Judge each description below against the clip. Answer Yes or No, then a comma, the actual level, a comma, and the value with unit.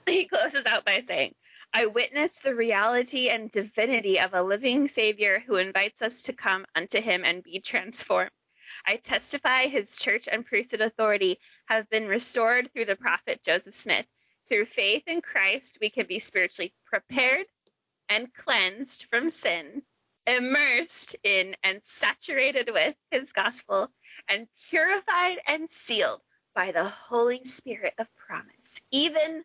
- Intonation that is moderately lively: No, wide, 6.6 semitones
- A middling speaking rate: Yes, average, 145 wpm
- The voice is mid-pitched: No, high, 245 Hz